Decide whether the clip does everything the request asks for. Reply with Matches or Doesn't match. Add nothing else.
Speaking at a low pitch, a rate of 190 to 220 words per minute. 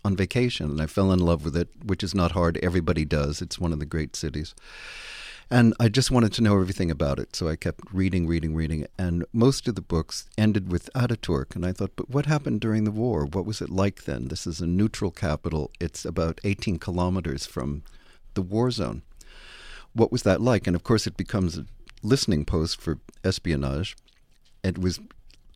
Matches